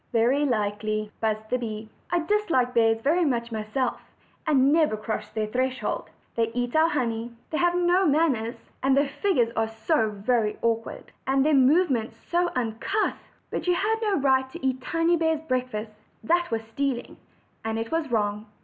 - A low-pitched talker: No, very high, 255 Hz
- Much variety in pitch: Yes, wide, 5.8 semitones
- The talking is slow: No, average, 175 wpm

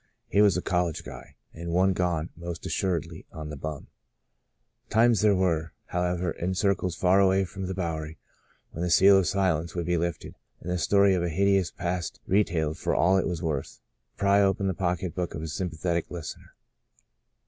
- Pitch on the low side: Yes, very low, 90 Hz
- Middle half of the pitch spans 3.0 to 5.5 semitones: No, narrow, 2.6 semitones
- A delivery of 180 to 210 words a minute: Yes, average, 190 wpm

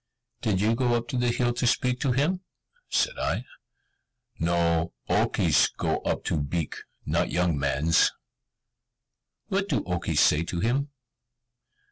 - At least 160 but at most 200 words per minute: No, slow, 135 wpm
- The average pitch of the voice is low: Yes, low, 115 Hz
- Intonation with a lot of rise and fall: Yes, wide, 7.1 semitones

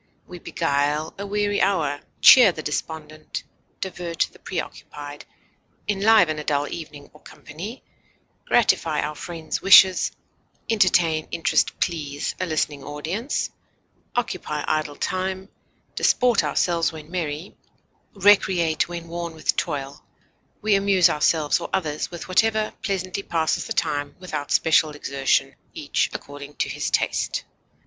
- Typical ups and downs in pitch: Yes, average, 4.1 semitones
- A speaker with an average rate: No, slow, 125 wpm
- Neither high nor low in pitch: Yes, medium, 165 Hz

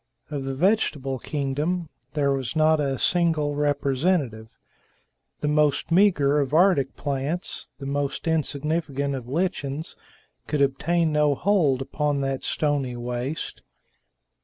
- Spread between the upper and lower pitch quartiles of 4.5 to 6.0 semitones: No, average, 2.7 semitones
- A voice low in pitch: No, medium, 145 Hz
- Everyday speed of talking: No, slow, 120 wpm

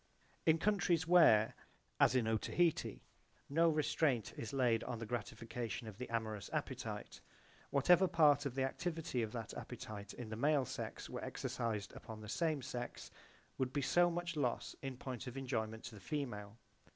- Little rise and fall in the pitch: No, wide, 5.5 semitones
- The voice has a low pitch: Yes, low, 125 Hz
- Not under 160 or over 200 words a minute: Yes, average, 170 wpm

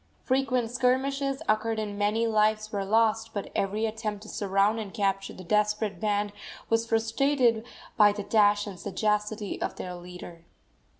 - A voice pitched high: Yes, high, 215 Hz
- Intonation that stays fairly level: Yes, narrow, 1.9 semitones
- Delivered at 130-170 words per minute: Yes, average, 155 wpm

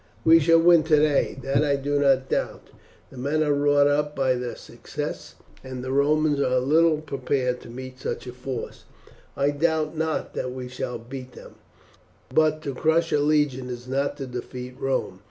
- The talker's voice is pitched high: No, medium, 140 Hz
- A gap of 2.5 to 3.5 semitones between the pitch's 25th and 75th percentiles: Yes, average, 3.0 semitones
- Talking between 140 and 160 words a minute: No, average, 180 wpm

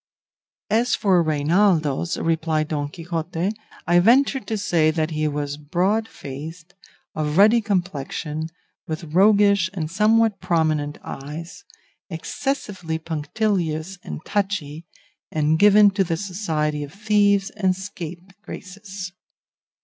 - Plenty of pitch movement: No, average, 4.5 semitones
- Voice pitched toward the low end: No, medium, 175 Hz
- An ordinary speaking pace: No, slow, 110 wpm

